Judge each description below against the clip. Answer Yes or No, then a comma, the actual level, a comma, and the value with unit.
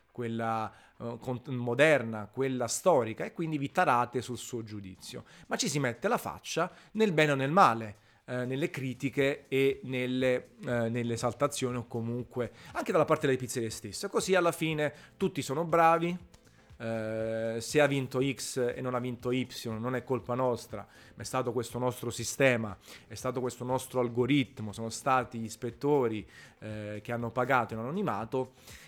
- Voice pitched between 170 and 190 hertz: No, low, 125 Hz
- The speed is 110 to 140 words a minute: No, average, 165 wpm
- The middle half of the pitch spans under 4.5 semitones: Yes, average, 2.8 semitones